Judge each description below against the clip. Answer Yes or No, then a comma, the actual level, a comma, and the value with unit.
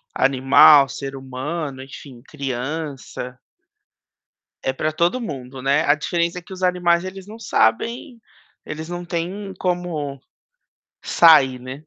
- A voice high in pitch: No, medium, 155 Hz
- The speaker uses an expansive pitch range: No, average, 4.8 semitones